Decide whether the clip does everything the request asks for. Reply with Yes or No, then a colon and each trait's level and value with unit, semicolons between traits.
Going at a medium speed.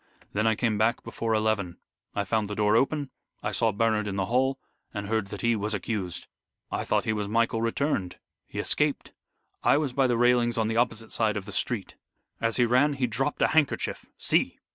No: fast, 210 wpm